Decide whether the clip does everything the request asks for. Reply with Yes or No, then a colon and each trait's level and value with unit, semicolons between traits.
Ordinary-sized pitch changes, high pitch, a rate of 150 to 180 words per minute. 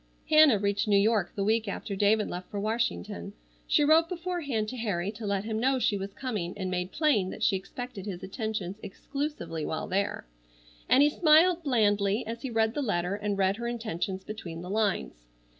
No: average, 4.2 semitones; high, 210 Hz; average, 190 wpm